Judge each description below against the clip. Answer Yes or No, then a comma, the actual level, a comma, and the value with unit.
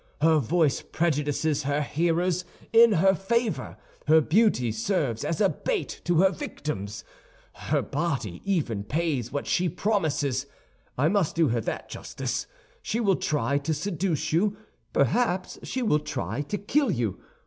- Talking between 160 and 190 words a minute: No, average, 145 wpm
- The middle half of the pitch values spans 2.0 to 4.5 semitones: No, wide, 5.4 semitones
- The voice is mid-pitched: Yes, medium, 160 Hz